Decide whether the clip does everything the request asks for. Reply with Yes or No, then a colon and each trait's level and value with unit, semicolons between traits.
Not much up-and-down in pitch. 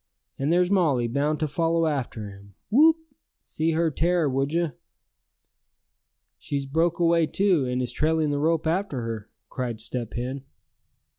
No: average, 4.6 semitones